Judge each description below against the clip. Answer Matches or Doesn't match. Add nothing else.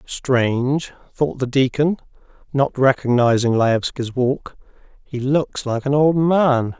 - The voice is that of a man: Matches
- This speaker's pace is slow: Matches